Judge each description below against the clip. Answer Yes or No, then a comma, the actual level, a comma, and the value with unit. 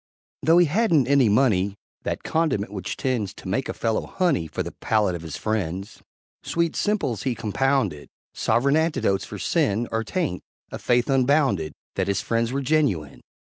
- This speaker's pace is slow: No, average, 170 wpm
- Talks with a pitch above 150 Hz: No, low, 115 Hz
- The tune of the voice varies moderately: No, wide, 6.2 semitones